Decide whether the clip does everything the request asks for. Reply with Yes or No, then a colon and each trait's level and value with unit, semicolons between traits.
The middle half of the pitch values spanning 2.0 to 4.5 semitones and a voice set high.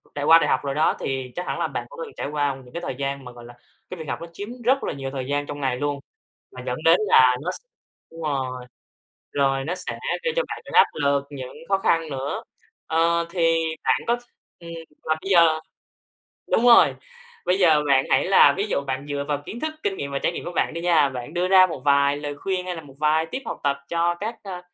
No: average, 4.2 semitones; medium, 150 Hz